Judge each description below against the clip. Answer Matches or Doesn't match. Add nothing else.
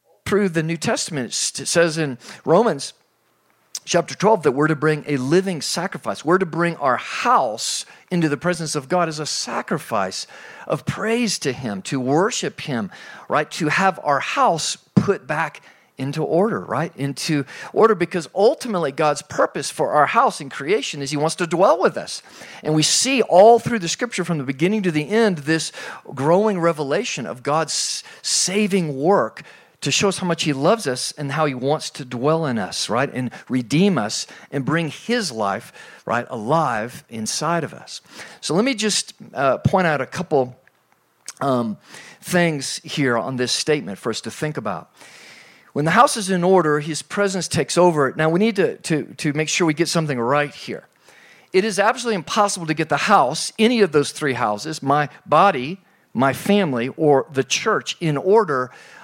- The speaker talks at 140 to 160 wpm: Doesn't match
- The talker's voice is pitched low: Doesn't match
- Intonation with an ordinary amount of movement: Matches